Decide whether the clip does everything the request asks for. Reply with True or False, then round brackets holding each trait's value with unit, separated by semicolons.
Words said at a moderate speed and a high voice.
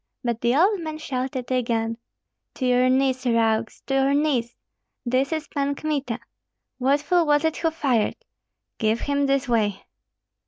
True (155 wpm; 265 Hz)